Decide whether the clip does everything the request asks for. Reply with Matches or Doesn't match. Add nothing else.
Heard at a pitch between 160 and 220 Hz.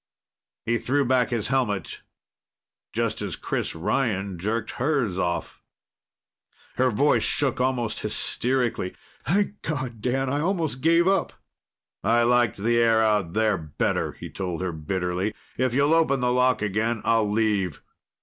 Doesn't match